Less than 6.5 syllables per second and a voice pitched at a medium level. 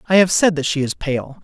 Yes: 5.4 syllables/s; medium, 160 Hz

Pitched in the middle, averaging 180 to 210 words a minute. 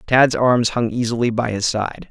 No: low, 115 Hz; average, 200 wpm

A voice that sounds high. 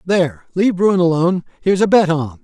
No: medium, 175 Hz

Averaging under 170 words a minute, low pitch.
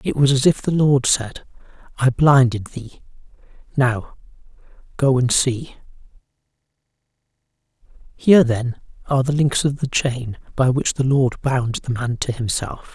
Yes: average, 145 wpm; low, 130 Hz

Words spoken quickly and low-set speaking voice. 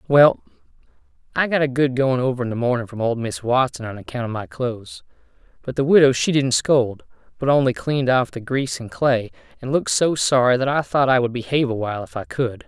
Yes: fast, 225 wpm; low, 125 Hz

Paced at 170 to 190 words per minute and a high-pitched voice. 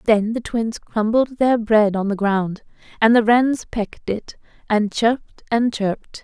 Yes: average, 175 wpm; high, 220 Hz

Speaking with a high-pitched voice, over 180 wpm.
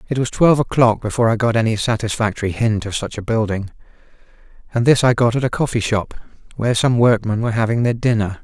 No: low, 115 Hz; fast, 205 wpm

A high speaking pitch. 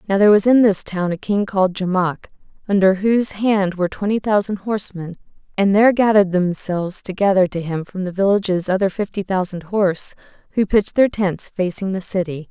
Yes: high, 195 Hz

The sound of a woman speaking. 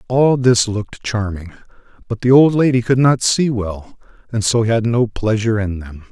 No: male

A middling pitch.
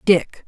Yes: medium, 170 Hz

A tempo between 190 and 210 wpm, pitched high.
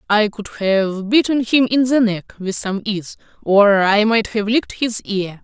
Yes: average, 200 wpm; high, 215 Hz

